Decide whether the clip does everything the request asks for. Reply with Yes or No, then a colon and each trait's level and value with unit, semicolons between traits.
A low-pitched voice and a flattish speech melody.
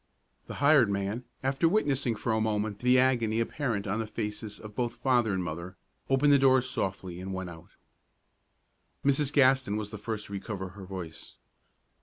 No: low, 110 Hz; average, 4.7 semitones